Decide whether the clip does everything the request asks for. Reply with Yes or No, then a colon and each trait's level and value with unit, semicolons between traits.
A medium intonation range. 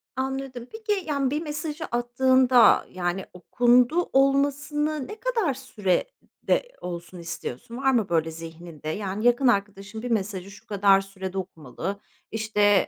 No: wide, 6.1 semitones